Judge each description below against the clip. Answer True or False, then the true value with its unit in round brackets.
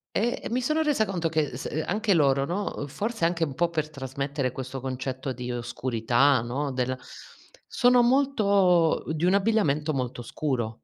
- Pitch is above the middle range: False (150 Hz)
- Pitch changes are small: False (7.4 semitones)